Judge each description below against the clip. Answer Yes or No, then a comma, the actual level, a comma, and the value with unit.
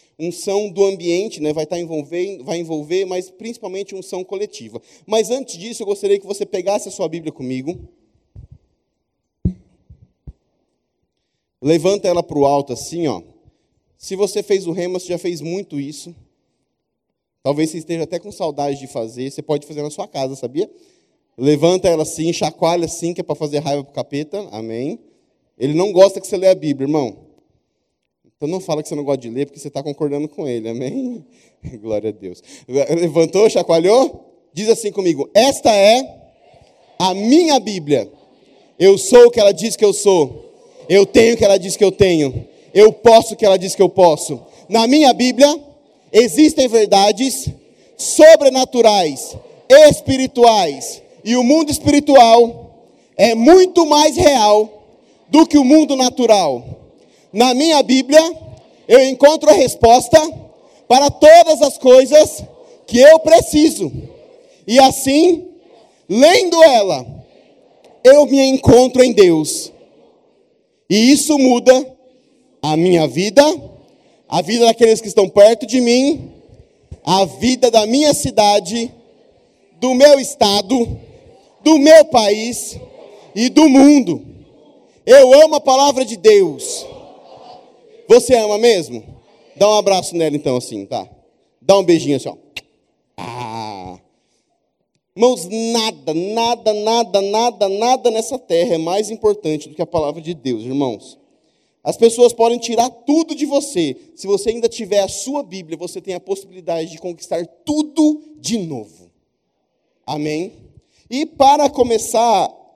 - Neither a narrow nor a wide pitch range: No, wide, 8.4 semitones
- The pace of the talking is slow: No, average, 145 wpm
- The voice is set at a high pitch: Yes, high, 210 Hz